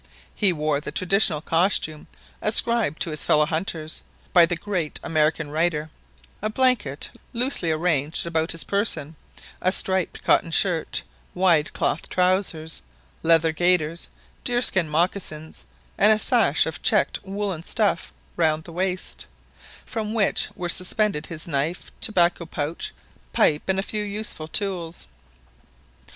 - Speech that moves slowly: Yes, slow, 130 wpm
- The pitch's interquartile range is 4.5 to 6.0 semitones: No, average, 3.8 semitones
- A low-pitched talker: No, medium, 170 Hz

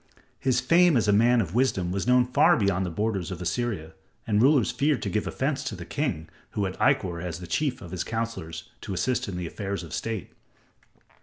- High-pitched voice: No, low, 105 Hz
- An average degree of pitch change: No, wide, 5.9 semitones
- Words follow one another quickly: Yes, fast, 215 wpm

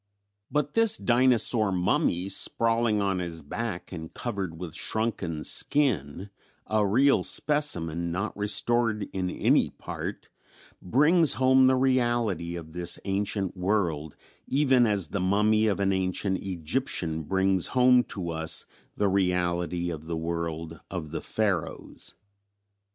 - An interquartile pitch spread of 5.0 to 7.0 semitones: Yes, wide, 5.4 semitones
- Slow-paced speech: Yes, slow, 130 wpm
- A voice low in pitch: Yes, very low, 95 Hz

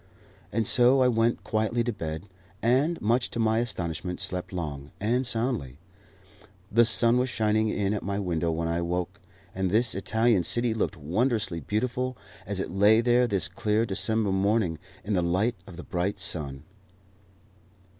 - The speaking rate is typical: Yes, average, 165 wpm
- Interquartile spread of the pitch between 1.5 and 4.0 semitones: No, average, 4.6 semitones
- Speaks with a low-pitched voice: Yes, low, 105 Hz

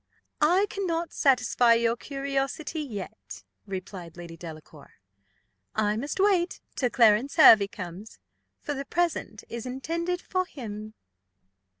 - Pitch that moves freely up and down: Yes, wide, 7.3 semitones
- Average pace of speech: No, slow, 115 wpm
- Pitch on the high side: Yes, very high, 250 Hz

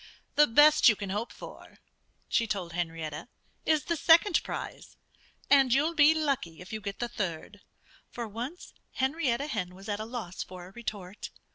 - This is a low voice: No, high, 225 Hz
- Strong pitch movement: Yes, wide, 7.1 semitones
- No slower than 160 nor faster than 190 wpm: Yes, average, 170 wpm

